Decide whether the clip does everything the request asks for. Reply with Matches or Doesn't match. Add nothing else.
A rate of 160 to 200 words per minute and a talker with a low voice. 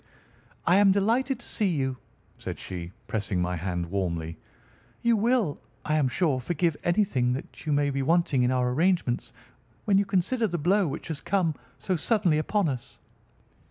Doesn't match